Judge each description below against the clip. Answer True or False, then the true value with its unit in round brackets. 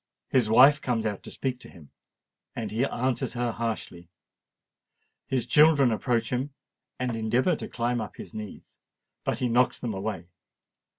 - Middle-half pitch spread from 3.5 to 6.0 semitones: False (2.6 semitones)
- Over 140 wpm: True (150 wpm)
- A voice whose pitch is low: True (120 Hz)